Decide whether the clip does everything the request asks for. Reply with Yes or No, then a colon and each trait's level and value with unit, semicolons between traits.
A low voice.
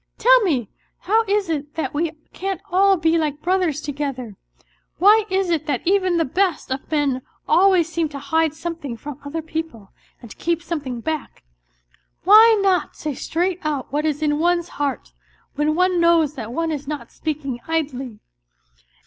No: very high, 320 Hz